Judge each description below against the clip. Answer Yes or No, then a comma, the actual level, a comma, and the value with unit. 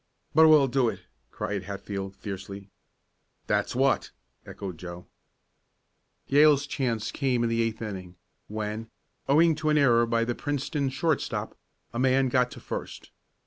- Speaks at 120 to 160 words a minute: Yes, average, 145 wpm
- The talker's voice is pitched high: No, low, 120 Hz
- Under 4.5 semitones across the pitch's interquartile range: No, wide, 5.4 semitones